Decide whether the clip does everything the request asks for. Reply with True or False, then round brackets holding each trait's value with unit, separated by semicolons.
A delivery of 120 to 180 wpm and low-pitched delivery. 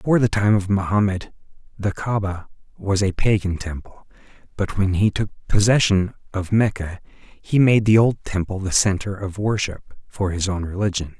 True (170 wpm; 100 Hz)